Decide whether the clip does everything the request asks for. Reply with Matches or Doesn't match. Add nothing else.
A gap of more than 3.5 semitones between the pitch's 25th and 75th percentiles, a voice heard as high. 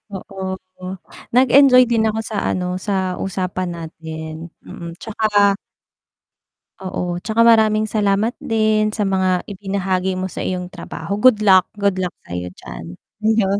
Doesn't match